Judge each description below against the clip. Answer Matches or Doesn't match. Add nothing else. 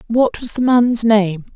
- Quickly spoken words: Doesn't match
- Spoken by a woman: Matches